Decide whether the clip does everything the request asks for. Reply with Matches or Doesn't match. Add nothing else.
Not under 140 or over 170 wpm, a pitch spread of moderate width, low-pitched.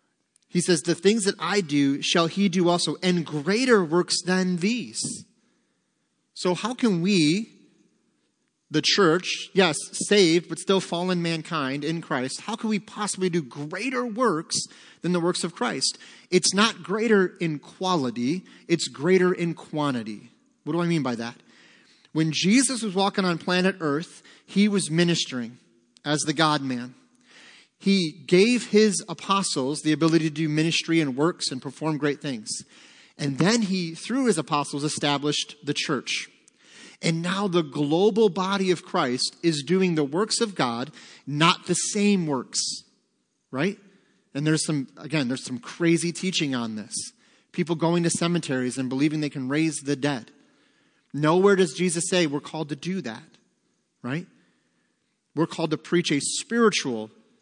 Doesn't match